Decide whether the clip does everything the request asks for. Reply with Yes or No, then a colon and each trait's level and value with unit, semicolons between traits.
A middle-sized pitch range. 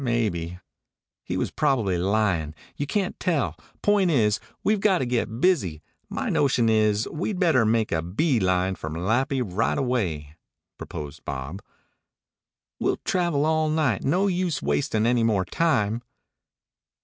No: wide, 8.5 semitones